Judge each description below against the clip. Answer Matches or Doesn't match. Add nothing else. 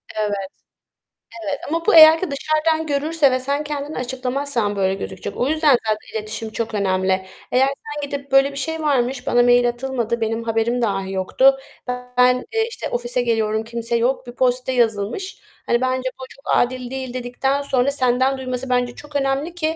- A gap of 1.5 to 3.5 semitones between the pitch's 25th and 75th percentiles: Matches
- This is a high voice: Matches